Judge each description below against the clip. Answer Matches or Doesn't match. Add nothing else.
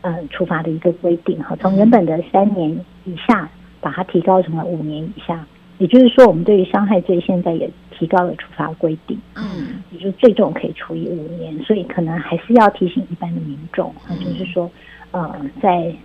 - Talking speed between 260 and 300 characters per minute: Matches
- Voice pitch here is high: Doesn't match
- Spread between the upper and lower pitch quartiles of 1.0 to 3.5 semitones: Matches